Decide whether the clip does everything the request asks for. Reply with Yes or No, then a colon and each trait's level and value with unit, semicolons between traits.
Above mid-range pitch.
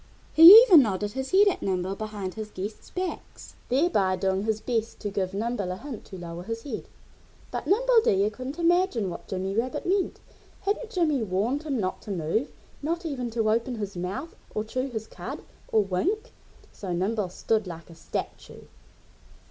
Yes: high, 220 Hz